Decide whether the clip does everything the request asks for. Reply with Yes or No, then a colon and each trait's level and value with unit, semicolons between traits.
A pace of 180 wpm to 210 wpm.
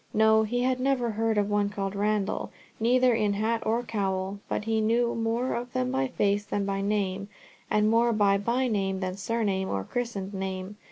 Yes: average, 185 wpm